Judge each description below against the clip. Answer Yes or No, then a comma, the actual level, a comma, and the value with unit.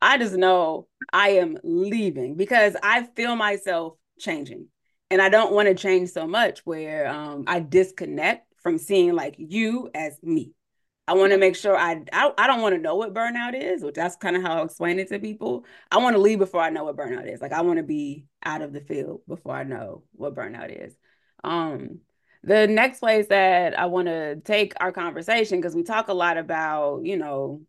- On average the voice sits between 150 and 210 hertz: Yes, medium, 185 Hz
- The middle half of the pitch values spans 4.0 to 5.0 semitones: Yes, average, 4.3 semitones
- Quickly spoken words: Yes, fast, 210 wpm